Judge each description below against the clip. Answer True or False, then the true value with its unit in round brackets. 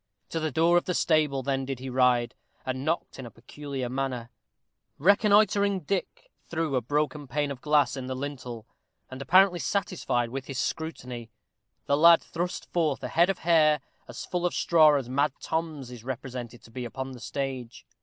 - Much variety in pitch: False (4.3 semitones)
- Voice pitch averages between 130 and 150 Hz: True (140 Hz)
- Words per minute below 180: False (185 wpm)